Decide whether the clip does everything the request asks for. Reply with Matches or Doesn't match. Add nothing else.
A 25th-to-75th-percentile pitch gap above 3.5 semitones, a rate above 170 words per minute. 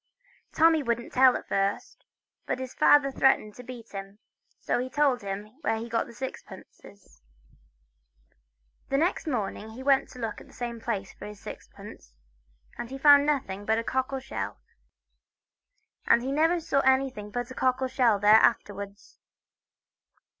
Doesn't match